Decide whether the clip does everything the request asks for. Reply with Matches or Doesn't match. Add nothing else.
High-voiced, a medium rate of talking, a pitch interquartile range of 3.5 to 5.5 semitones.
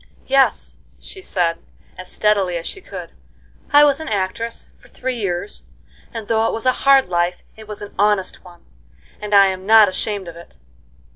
Matches